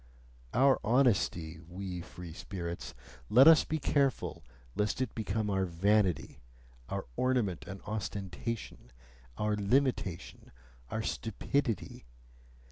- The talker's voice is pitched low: Yes, low, 105 Hz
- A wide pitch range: Yes, wide, 5.7 semitones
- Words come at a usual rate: No, slow, 105 wpm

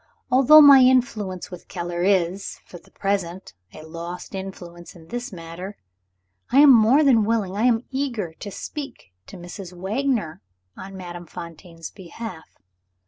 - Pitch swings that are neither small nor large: No, wide, 5.7 semitones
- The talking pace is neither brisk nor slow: Yes, average, 145 wpm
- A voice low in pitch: No, high, 195 Hz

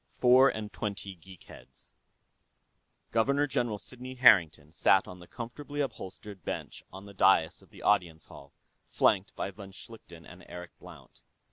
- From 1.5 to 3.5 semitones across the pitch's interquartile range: No, average, 5.0 semitones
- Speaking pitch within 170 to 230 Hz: No, low, 100 Hz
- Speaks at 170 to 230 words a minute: No, average, 155 wpm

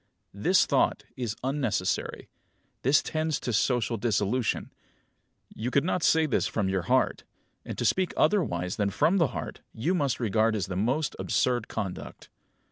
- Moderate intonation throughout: No, wide, 6.1 semitones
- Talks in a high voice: No, low, 120 Hz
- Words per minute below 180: Yes, average, 155 wpm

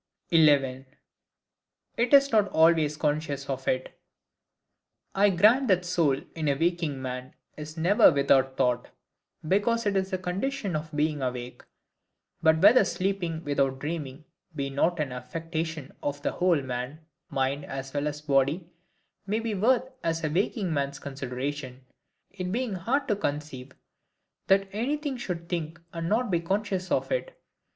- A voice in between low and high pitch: Yes, medium, 160 Hz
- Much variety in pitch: Yes, wide, 5.7 semitones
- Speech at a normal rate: Yes, average, 150 wpm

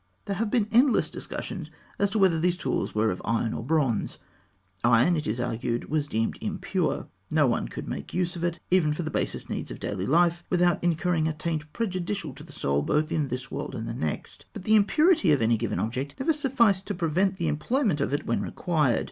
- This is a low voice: No, medium, 160 Hz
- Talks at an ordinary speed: No, fast, 220 wpm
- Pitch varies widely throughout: Yes, wide, 6.4 semitones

